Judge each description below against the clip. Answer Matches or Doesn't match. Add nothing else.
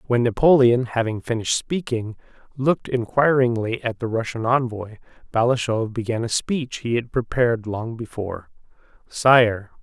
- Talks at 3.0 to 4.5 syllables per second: Doesn't match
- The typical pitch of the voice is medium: Doesn't match